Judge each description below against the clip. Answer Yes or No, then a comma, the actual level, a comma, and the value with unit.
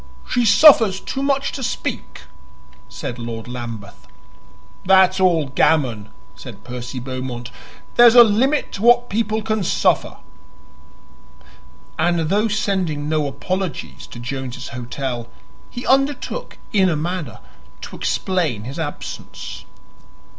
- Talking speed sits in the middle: No, slow, 120 wpm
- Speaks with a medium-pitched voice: Yes, medium, 170 Hz